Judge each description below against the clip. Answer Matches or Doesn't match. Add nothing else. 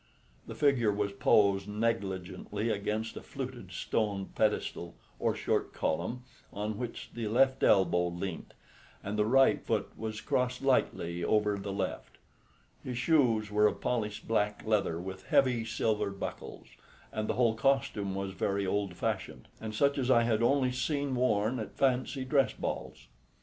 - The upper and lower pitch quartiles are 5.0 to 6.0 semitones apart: Doesn't match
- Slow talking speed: Doesn't match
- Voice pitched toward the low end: Matches